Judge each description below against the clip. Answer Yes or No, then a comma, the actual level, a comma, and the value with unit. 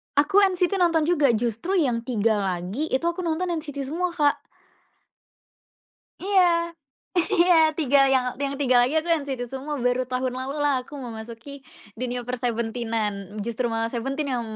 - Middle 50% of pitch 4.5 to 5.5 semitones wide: Yes, average, 5.2 semitones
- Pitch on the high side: Yes, very high, 265 Hz